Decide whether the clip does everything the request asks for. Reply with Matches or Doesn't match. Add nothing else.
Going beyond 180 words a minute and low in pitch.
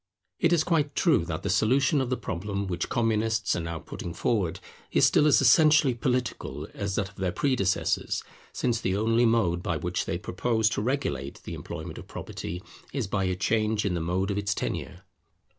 Matches